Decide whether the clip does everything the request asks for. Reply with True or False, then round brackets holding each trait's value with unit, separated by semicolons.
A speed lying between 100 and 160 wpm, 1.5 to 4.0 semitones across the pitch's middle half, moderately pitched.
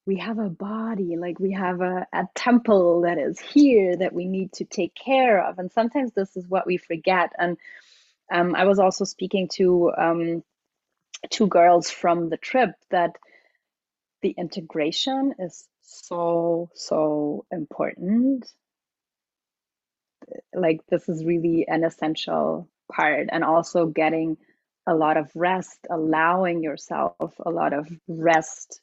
True (140 wpm; 2.5 semitones; 175 Hz)